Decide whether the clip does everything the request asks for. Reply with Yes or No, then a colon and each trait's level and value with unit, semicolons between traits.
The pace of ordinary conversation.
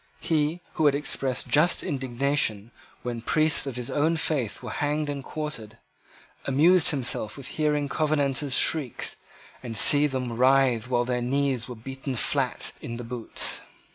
Yes: average, 155 wpm